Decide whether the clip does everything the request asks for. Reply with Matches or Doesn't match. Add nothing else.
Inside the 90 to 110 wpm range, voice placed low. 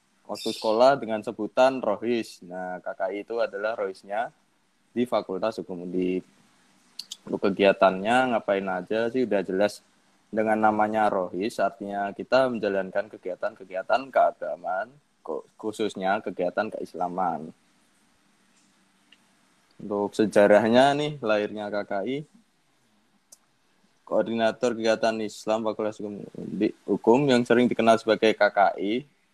Matches